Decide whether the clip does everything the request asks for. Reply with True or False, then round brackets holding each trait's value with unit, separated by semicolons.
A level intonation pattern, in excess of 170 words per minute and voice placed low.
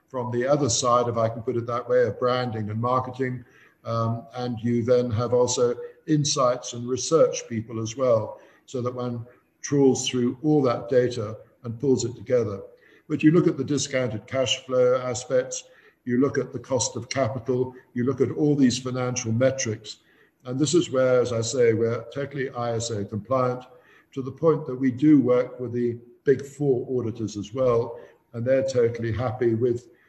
True (2.1 semitones; 185 wpm; 125 Hz)